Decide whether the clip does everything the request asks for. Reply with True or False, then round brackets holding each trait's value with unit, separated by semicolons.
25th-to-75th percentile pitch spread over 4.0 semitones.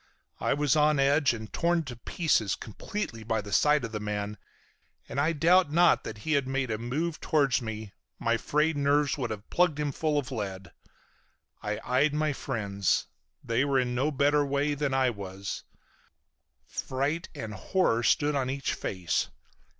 True (5.2 semitones)